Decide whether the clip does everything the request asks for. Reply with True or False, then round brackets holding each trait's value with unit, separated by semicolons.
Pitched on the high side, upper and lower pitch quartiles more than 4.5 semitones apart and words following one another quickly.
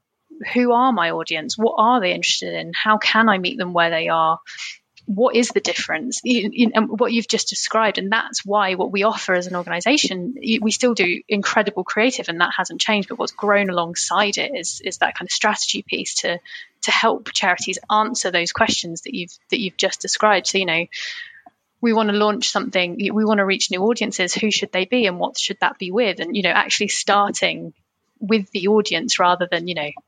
False (205 Hz; 3.8 semitones; 215 wpm)